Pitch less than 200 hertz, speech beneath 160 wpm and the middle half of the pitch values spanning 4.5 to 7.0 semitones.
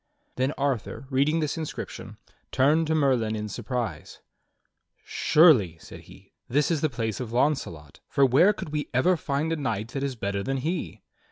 No: low, 135 Hz; average, 170 wpm; average, 5.0 semitones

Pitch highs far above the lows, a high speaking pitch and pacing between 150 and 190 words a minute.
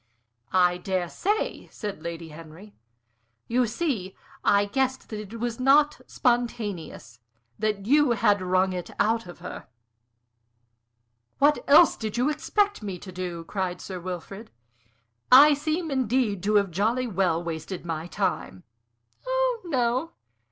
No: wide, 6.2 semitones; high, 210 Hz; slow, 135 wpm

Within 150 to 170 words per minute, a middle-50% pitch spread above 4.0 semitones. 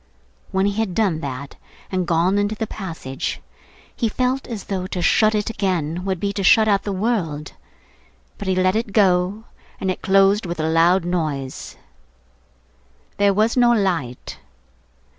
No: average, 160 wpm; average, 3.5 semitones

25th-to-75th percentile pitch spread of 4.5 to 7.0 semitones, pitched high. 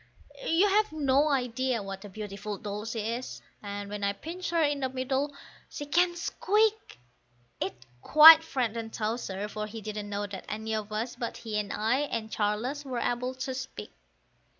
Yes: average, 5.2 semitones; high, 235 Hz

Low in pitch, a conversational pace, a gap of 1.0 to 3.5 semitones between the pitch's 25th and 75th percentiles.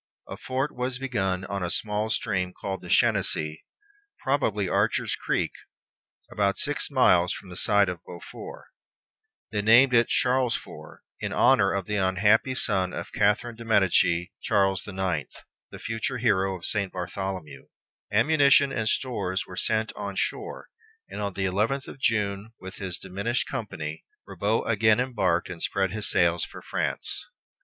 No: low, 100 Hz; average, 155 wpm; average, 3.9 semitones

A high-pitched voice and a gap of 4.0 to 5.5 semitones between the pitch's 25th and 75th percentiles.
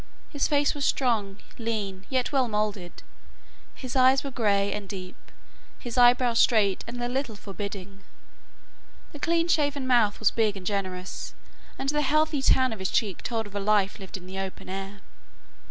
Yes: high, 220 Hz; average, 4.8 semitones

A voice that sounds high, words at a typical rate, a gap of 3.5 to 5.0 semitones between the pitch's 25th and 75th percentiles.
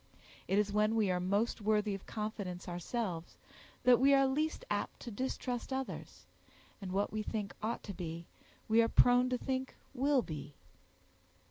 Yes: high, 215 Hz; average, 165 wpm; average, 4.3 semitones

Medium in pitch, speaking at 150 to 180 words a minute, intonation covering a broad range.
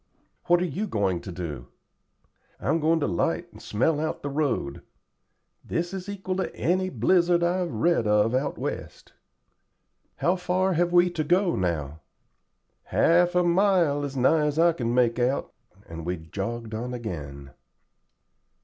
Yes: medium, 145 Hz; average, 155 wpm; wide, 8.5 semitones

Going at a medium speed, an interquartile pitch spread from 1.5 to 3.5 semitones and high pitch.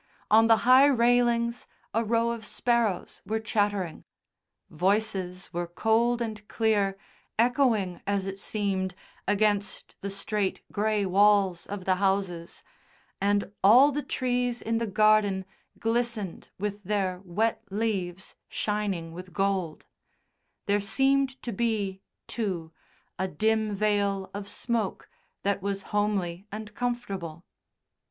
No: slow, 120 wpm; average, 2.9 semitones; high, 205 Hz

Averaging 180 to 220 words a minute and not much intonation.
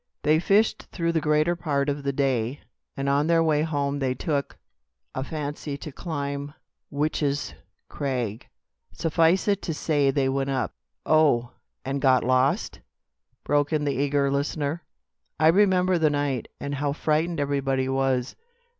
No: average, 155 wpm; narrow, 2.3 semitones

